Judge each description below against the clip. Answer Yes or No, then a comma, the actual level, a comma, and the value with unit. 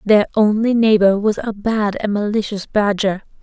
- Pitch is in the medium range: No, high, 210 Hz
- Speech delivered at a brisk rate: No, average, 160 wpm